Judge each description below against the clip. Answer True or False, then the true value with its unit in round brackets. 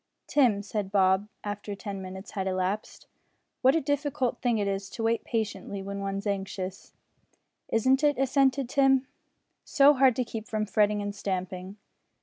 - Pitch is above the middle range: True (210 Hz)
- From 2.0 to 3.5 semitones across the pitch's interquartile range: False (4.7 semitones)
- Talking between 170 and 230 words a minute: False (155 wpm)